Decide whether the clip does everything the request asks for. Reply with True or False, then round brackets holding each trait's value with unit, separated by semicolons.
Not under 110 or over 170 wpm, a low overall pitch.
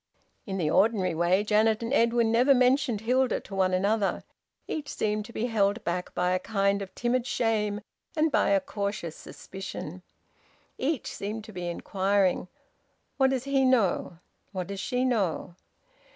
False (160 wpm; 210 Hz)